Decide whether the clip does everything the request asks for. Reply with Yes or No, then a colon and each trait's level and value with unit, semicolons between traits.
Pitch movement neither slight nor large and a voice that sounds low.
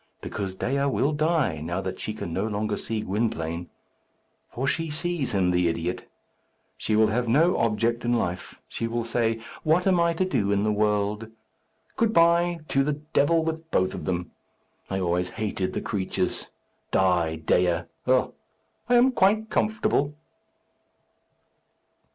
No: wide, 8.6 semitones; low, 115 Hz